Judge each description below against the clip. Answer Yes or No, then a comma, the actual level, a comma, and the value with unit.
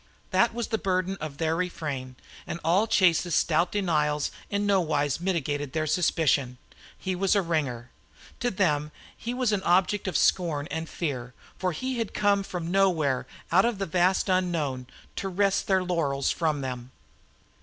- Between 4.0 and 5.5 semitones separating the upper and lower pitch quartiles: Yes, average, 4.5 semitones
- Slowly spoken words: No, average, 165 wpm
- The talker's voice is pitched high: No, medium, 170 Hz